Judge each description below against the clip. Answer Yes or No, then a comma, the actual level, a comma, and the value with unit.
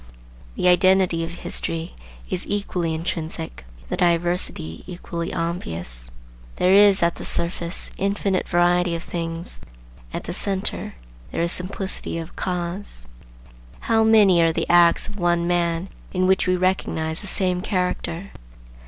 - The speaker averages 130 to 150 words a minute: Yes, slow, 135 wpm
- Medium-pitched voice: Yes, medium, 175 Hz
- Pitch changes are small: Yes, narrow, 2.0 semitones